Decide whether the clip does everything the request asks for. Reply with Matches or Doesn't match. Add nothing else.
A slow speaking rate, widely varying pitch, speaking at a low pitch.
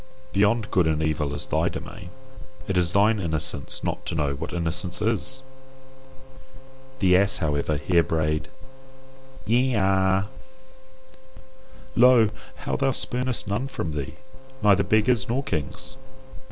Matches